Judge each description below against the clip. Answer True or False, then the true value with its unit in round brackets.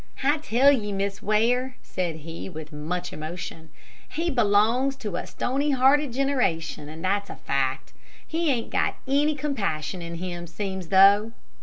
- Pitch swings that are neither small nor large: False (7.6 semitones)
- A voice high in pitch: True (205 Hz)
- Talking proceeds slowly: False (155 wpm)